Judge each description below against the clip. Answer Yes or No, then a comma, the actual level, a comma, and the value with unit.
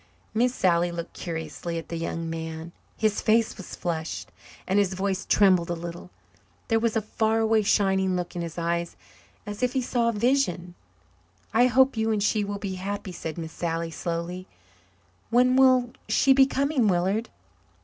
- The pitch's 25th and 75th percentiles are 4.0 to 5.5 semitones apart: Yes, average, 4.8 semitones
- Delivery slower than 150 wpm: No, average, 175 wpm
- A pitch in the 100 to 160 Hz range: No, high, 195 Hz